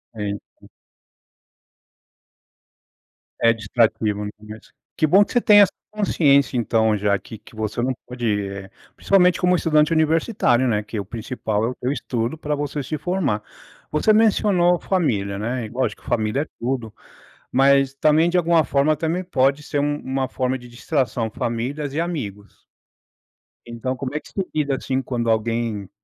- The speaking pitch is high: No, low, 130 Hz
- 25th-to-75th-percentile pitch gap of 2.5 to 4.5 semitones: No, wide, 5.6 semitones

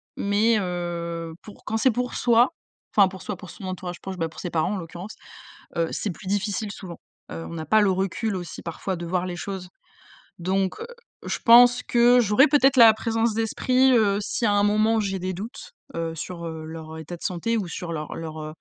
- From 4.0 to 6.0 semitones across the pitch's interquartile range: Yes, average, 4.5 semitones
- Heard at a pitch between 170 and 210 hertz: Yes, high, 190 Hz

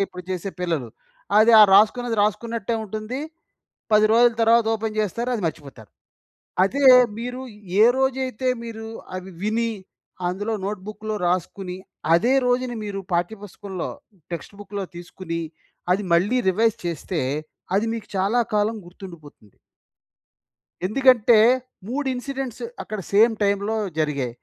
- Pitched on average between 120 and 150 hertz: No, high, 210 Hz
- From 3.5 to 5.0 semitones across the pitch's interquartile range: Yes, average, 4.1 semitones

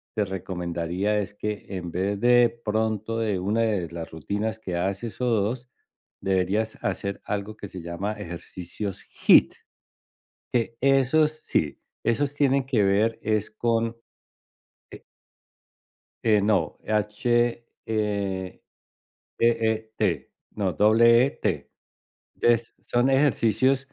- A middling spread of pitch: Yes, average, 3.1 semitones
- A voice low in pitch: Yes, low, 110 Hz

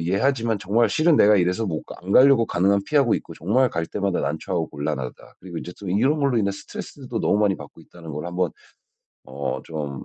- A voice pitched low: Yes, very low, 95 Hz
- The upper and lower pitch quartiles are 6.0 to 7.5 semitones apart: No, wide, 5.6 semitones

